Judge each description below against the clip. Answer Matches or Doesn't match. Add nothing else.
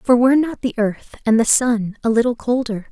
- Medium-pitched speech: Doesn't match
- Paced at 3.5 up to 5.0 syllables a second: Doesn't match